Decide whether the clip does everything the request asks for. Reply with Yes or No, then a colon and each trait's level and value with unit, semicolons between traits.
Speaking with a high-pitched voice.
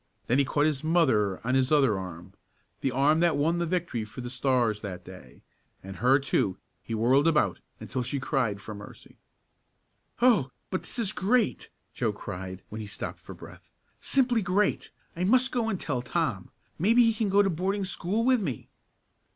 No: medium, 140 Hz